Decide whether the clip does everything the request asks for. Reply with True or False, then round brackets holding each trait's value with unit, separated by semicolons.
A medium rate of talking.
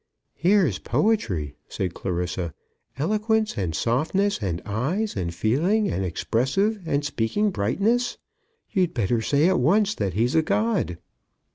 False (130 wpm)